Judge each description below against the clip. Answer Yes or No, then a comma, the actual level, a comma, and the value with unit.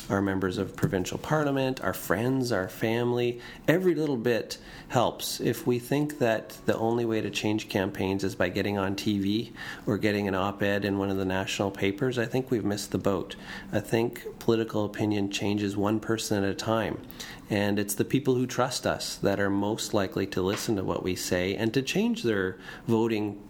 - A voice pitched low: Yes, low, 105 Hz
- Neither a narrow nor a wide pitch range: Yes, average, 3.3 semitones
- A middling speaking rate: Yes, average, 195 wpm